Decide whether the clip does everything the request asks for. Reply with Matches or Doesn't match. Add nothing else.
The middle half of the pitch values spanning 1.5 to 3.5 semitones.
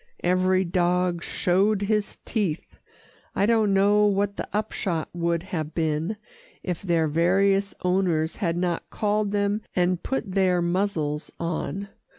Matches